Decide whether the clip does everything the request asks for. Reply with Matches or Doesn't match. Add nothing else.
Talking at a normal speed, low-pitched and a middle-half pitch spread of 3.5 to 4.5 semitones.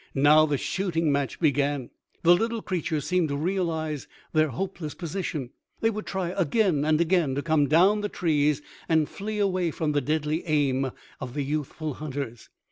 Doesn't match